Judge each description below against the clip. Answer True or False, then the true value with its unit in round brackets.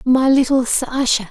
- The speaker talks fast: False (140 wpm)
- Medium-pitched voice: False (255 Hz)